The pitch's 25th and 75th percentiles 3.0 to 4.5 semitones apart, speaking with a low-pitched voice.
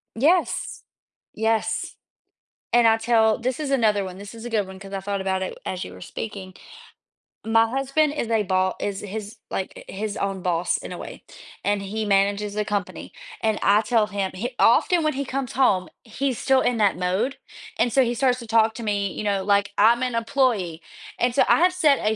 No: average, 3.4 semitones; high, 220 Hz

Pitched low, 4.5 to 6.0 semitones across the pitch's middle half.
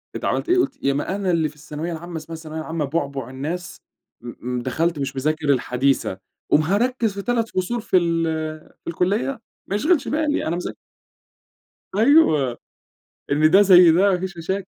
No: medium, 170 Hz; average, 5.0 semitones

